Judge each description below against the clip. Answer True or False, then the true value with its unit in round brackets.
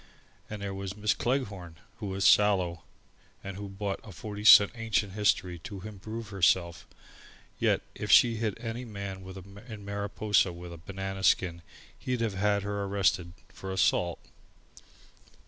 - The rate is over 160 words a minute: False (150 wpm)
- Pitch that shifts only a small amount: True (1.9 semitones)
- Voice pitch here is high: False (100 Hz)